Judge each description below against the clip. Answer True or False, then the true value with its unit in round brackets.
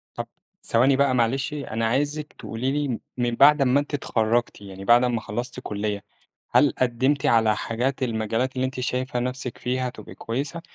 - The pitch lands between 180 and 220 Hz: False (125 Hz)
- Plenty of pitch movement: False (2.7 semitones)